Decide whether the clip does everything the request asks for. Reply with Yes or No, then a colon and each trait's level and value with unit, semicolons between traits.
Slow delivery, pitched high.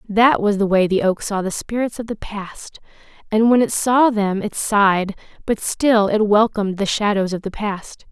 No: fast, 205 wpm; high, 210 Hz